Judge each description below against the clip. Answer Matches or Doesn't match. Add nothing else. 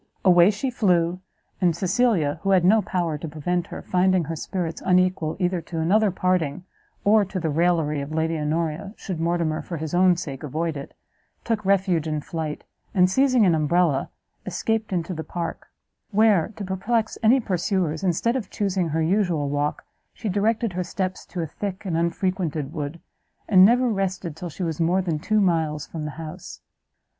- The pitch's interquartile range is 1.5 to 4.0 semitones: Matches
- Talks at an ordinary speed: Matches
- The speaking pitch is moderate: Matches